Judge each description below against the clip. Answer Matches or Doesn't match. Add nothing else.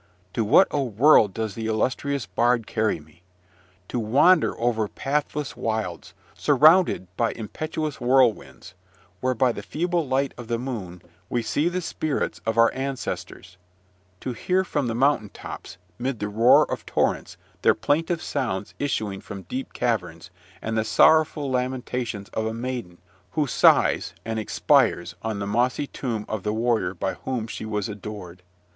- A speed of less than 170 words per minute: Matches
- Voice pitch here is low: Matches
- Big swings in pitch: Doesn't match